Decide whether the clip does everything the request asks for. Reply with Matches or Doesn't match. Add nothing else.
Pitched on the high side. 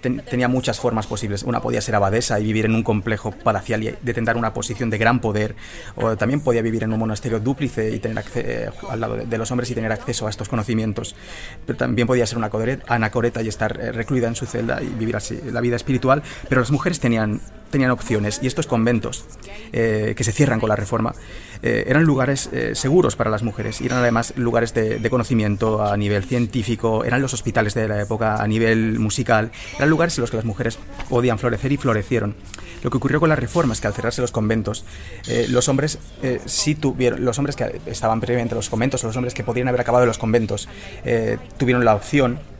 Doesn't match